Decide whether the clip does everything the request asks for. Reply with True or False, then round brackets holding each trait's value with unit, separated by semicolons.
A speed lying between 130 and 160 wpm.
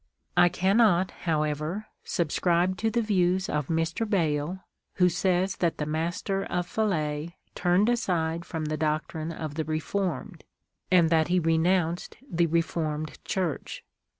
True (140 wpm)